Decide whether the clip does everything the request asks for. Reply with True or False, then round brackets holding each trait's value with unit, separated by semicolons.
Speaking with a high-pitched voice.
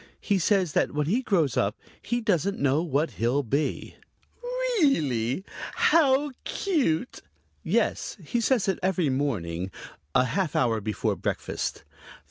False (165 Hz)